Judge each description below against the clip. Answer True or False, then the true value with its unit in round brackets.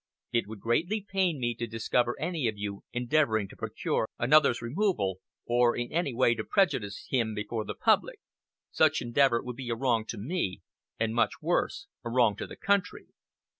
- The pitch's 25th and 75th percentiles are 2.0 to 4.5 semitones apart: False (5.3 semitones)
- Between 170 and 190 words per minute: True (180 wpm)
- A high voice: False (120 Hz)